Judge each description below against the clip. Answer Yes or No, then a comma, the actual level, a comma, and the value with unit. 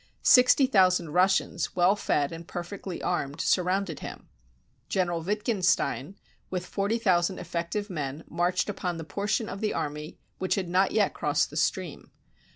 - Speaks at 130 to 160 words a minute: Yes, average, 150 wpm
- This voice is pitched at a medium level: Yes, medium, 180 Hz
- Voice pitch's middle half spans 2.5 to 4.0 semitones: Yes, average, 2.8 semitones